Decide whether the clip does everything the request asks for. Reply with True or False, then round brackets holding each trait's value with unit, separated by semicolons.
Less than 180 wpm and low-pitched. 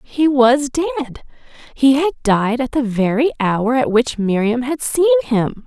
False (160 wpm; 260 Hz)